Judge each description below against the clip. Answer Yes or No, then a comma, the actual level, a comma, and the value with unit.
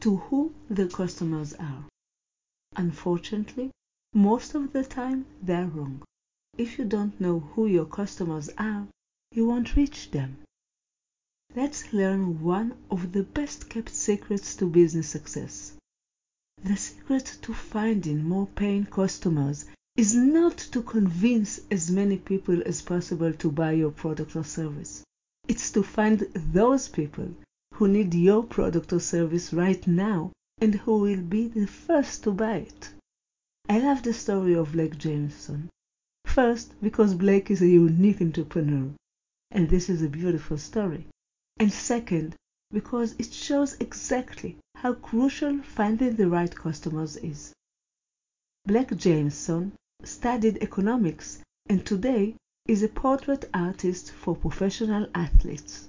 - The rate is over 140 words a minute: No, slow, 135 wpm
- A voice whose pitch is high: Yes, high, 195 Hz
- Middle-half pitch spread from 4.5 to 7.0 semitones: Yes, average, 5.0 semitones